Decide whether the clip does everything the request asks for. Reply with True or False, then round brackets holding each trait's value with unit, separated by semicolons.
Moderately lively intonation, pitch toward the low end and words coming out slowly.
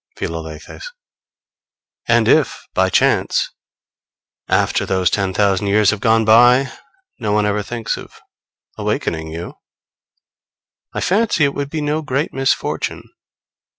False (6.1 semitones; 110 Hz; 120 wpm)